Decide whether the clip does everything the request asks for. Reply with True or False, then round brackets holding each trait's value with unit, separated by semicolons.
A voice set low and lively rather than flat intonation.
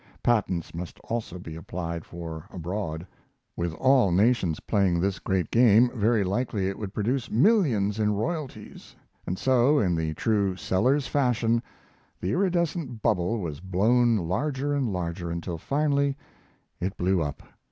True (105 Hz; 5.8 semitones)